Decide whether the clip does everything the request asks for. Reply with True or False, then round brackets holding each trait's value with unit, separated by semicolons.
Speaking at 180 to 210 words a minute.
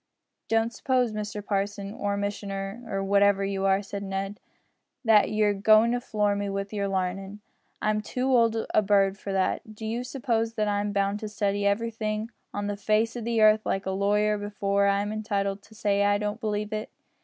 True (190 wpm)